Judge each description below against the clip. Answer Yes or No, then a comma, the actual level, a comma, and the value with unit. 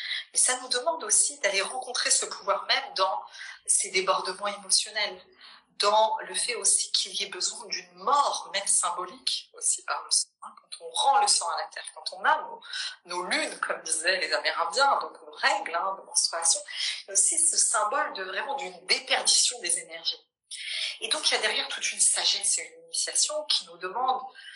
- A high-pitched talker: Yes, very high, 285 Hz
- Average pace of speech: Yes, average, 195 wpm